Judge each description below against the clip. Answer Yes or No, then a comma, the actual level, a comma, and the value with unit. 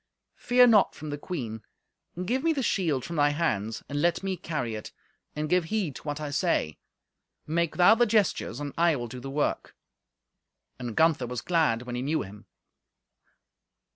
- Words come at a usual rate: Yes, average, 180 wpm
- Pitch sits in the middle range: Yes, medium, 155 Hz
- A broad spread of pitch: Yes, wide, 6.2 semitones